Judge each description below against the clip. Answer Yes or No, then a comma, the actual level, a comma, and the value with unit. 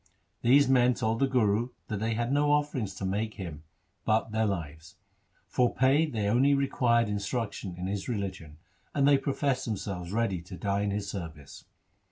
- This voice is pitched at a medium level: No, low, 110 Hz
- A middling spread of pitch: Yes, average, 4.5 semitones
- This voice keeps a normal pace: Yes, average, 175 wpm